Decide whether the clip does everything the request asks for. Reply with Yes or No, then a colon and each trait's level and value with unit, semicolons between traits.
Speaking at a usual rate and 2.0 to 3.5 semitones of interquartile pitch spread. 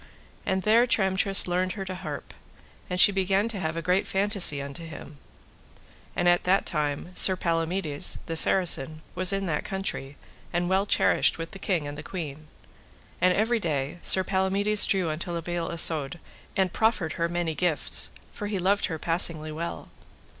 Yes: average, 175 wpm; average, 3.1 semitones